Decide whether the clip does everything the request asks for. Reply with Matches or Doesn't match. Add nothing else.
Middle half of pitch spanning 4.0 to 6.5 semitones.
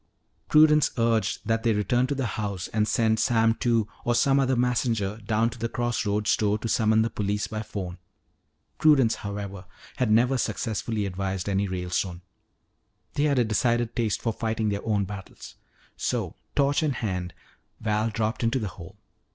Doesn't match